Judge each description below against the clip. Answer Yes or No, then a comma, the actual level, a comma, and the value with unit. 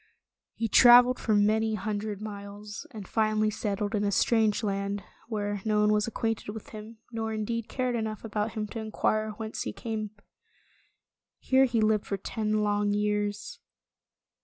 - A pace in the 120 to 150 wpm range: No, average, 160 wpm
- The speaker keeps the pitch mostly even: Yes, narrow, 1.3 semitones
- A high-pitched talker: Yes, high, 215 Hz